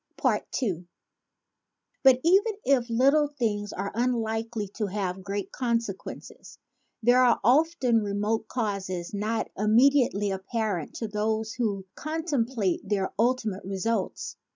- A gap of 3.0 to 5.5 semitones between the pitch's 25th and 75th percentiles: Yes, average, 3.8 semitones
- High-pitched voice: Yes, high, 220 Hz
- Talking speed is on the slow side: Yes, slow, 110 wpm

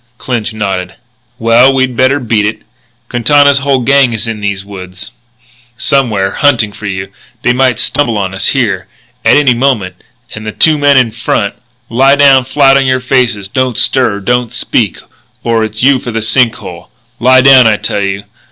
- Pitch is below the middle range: Yes, low, 120 Hz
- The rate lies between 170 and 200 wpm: Yes, average, 185 wpm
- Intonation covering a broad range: No, average, 4.1 semitones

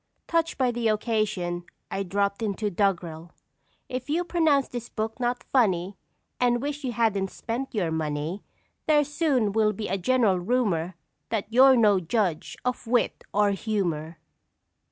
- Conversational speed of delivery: Yes, average, 150 wpm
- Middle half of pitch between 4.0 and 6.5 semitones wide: Yes, average, 4.8 semitones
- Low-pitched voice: No, high, 215 Hz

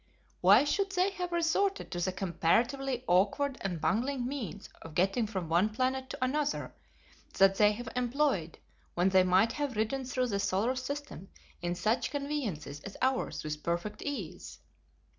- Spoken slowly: No, average, 160 wpm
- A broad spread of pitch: Yes, wide, 6.8 semitones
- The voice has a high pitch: Yes, high, 230 Hz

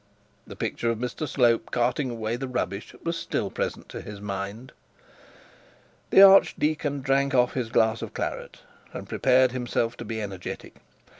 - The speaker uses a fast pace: No, average, 155 wpm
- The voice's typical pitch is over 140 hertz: No, low, 120 Hz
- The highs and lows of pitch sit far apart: No, average, 3.2 semitones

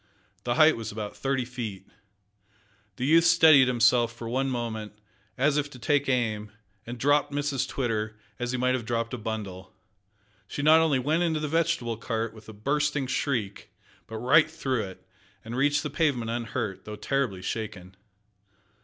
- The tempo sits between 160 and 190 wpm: Yes, average, 170 wpm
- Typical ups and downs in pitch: Yes, average, 4.6 semitones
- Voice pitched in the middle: No, low, 125 Hz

